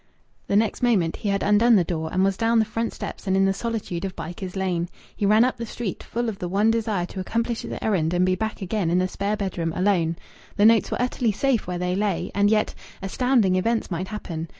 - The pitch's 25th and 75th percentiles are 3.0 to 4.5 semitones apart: Yes, average, 3.6 semitones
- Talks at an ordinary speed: No, fast, 240 wpm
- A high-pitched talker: Yes, high, 200 Hz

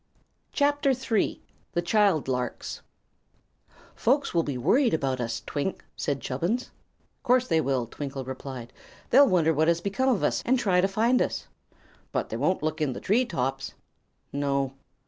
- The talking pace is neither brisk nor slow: Yes, average, 160 wpm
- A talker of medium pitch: Yes, medium, 165 Hz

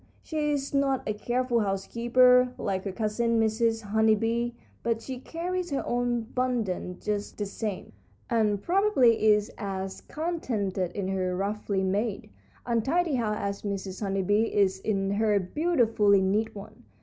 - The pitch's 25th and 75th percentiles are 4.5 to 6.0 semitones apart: No, average, 3.7 semitones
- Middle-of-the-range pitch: No, high, 220 Hz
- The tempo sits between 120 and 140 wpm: No, average, 150 wpm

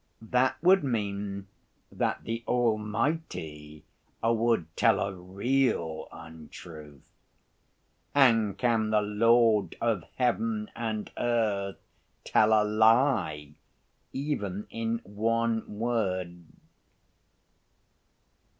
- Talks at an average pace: No, slow, 85 wpm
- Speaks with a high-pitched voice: No, low, 110 Hz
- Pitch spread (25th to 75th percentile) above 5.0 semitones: No, average, 3.3 semitones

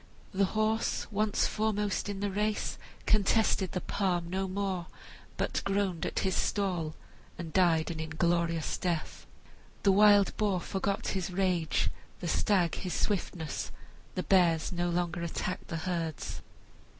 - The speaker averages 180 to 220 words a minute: No, average, 140 wpm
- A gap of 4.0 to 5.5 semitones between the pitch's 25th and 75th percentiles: No, average, 2.9 semitones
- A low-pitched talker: No, medium, 185 Hz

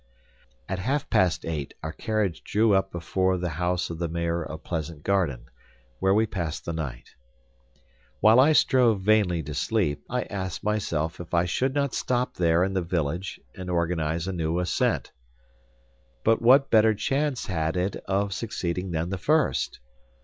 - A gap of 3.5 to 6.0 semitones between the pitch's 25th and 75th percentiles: Yes, average, 4.5 semitones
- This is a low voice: Yes, very low, 90 Hz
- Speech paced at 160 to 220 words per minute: Yes, average, 165 wpm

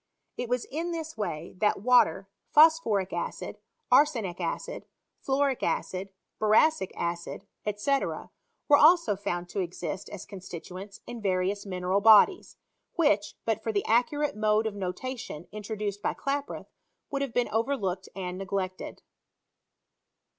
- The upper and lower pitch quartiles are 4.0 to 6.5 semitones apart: Yes, wide, 5.5 semitones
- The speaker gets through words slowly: Yes, slow, 125 wpm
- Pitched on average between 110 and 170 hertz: No, high, 210 Hz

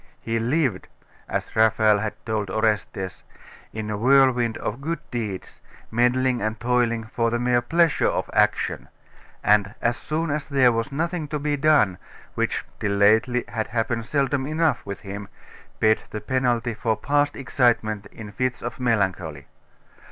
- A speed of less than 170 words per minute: Yes, average, 150 wpm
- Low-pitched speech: Yes, low, 120 Hz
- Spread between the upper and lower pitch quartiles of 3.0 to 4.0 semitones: Yes, average, 3.7 semitones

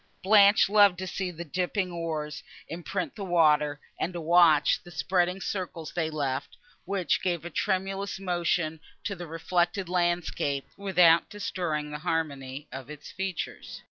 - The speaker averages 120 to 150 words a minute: Yes, average, 145 wpm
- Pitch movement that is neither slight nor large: Yes, average, 3.3 semitones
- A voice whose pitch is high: No, medium, 175 Hz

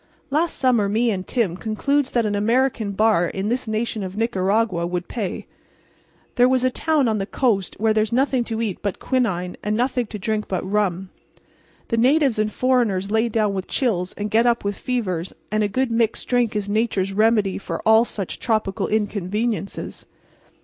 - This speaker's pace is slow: No, average, 185 wpm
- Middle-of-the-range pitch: No, high, 215 Hz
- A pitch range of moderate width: Yes, average, 3.3 semitones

